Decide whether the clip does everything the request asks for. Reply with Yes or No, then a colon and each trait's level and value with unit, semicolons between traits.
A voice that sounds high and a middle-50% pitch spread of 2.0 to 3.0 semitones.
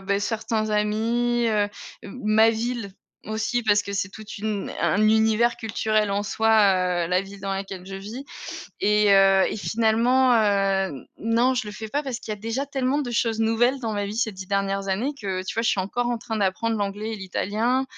Yes: high, 215 Hz; narrow, 2.5 semitones